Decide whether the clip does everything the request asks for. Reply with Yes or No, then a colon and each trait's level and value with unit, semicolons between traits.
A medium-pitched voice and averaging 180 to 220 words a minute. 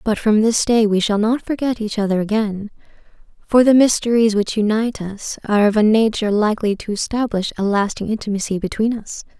No: high, 215 Hz; average, 185 wpm